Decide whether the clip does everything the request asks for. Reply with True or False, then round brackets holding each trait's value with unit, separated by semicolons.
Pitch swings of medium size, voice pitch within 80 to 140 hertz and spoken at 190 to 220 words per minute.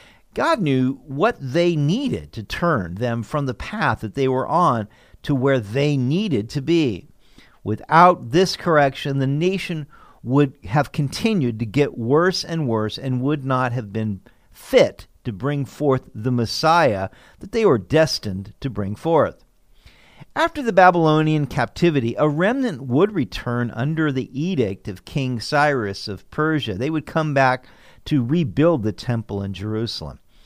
False (5.0 semitones; 135 Hz; 155 wpm)